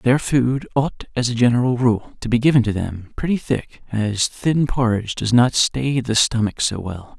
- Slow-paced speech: No, average, 200 wpm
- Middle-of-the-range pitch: No, low, 120 Hz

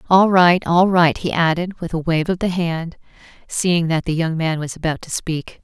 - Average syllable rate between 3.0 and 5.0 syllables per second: Yes, 4.7 syllables/s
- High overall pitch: No, medium, 170 Hz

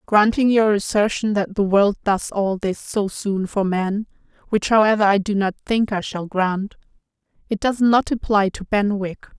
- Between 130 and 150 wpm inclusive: No, average, 180 wpm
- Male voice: No, female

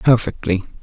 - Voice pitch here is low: Yes, low, 110 Hz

